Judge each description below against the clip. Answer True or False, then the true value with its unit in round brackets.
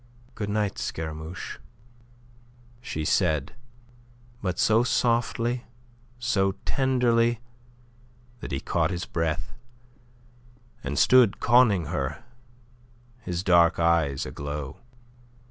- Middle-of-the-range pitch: False (90 Hz)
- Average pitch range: False (6.8 semitones)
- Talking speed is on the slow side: True (90 wpm)